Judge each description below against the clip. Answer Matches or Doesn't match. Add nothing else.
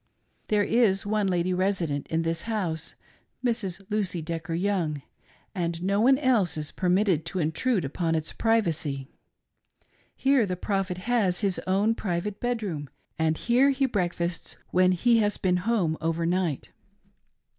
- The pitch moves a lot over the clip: Doesn't match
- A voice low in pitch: Doesn't match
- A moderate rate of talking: Matches